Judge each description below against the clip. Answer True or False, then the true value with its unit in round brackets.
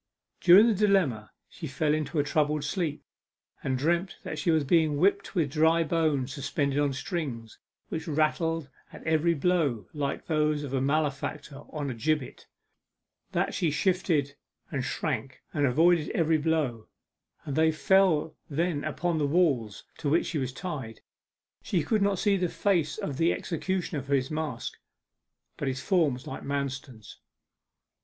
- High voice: False (155 Hz)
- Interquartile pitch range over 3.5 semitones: False (3.2 semitones)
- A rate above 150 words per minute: True (160 wpm)